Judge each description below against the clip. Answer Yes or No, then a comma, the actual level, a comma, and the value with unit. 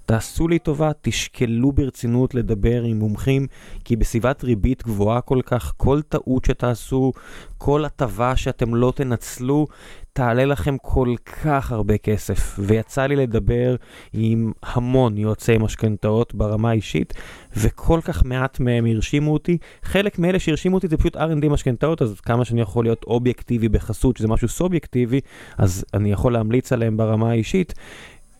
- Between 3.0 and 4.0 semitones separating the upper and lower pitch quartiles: Yes, average, 3.6 semitones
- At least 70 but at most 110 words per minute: No, average, 145 wpm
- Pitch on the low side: Yes, low, 125 Hz